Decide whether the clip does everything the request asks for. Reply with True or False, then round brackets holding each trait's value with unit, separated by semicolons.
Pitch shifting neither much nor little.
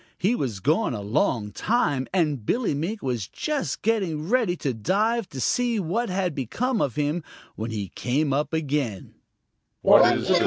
False (8.8 semitones)